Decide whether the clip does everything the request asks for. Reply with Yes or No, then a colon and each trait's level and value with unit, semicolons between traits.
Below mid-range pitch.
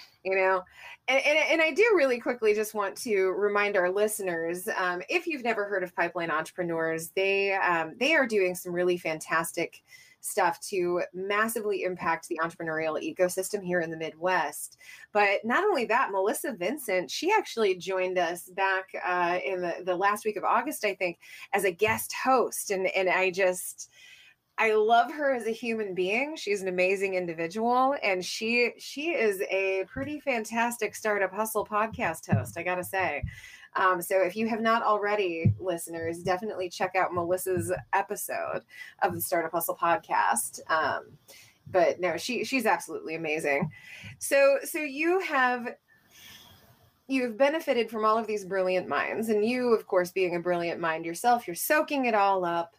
No: high, 195 Hz